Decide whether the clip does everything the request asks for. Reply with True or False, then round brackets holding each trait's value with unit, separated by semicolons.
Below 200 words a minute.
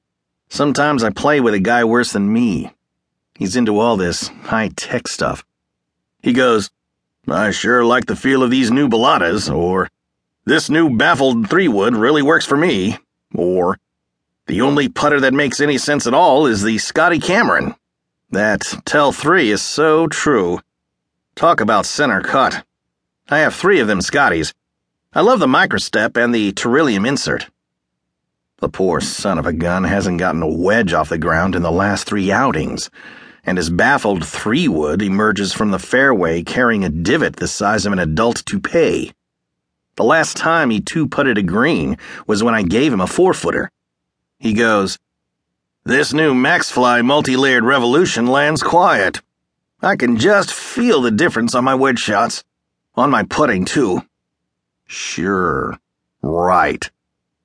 True (155 wpm)